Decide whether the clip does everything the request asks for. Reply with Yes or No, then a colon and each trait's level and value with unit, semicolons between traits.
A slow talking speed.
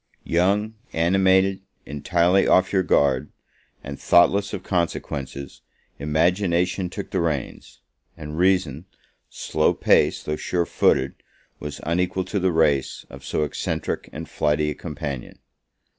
Yes: slow, 125 wpm